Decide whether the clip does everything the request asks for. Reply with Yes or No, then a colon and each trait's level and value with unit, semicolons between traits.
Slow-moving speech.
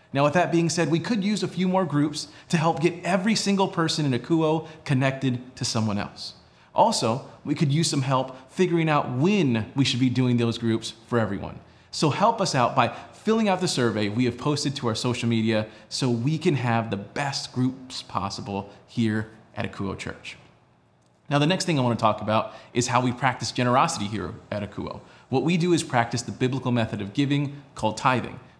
No: fast, 205 wpm